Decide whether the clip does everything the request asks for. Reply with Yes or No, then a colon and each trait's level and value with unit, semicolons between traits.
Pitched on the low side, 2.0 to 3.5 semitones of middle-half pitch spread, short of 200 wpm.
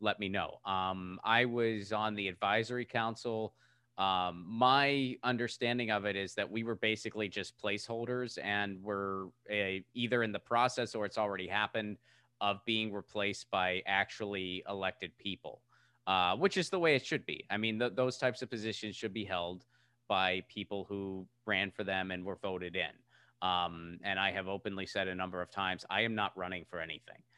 Yes: low, 105 Hz; average, 3.1 semitones; average, 185 wpm